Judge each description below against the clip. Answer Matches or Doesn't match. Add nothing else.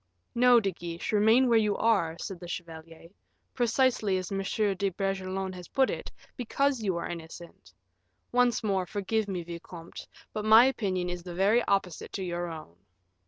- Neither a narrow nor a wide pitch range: Matches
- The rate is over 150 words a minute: Matches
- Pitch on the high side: Matches